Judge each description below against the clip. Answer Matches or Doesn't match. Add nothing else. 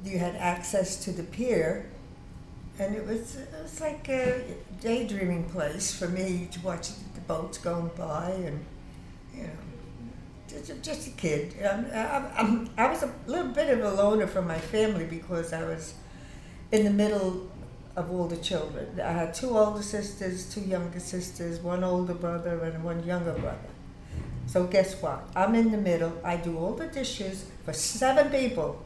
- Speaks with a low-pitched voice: Doesn't match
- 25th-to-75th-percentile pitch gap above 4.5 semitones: Doesn't match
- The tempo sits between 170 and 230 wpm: Matches